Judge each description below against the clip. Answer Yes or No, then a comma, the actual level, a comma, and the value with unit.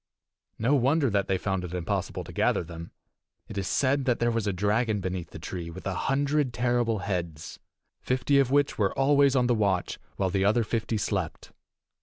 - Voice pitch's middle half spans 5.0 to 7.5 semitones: Yes, wide, 5.5 semitones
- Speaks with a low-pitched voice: Yes, low, 110 Hz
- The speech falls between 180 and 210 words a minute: Yes, average, 195 wpm